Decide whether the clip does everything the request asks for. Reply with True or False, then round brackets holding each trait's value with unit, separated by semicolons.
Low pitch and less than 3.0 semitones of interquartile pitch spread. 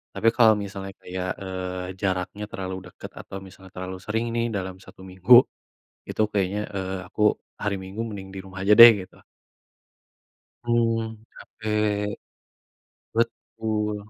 True (100 Hz; 2.6 semitones)